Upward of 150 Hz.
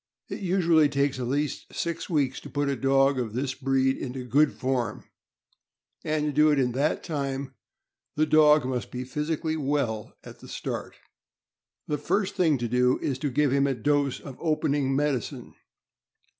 No: medium, 140 Hz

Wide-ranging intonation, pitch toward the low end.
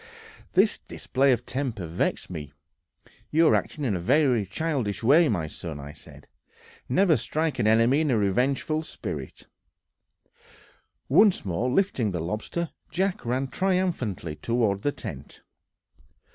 Yes: wide, 7.8 semitones; low, 125 Hz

